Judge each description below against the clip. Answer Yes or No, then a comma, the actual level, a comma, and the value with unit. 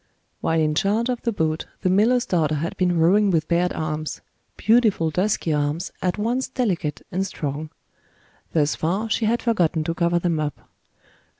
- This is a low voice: No, medium, 175 Hz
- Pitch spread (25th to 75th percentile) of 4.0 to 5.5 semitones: Yes, average, 5.0 semitones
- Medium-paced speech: Yes, average, 170 wpm